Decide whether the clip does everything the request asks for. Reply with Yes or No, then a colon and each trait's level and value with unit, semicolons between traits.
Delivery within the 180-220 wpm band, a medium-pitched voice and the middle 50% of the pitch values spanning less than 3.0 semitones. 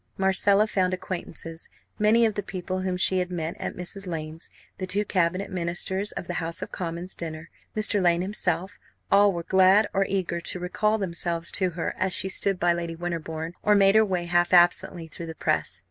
Yes: average, 195 wpm; medium, 180 Hz; narrow, 2.4 semitones